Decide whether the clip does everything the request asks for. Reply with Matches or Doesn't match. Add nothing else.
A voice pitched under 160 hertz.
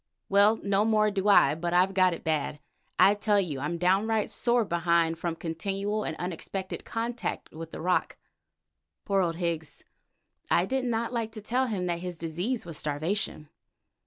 Doesn't match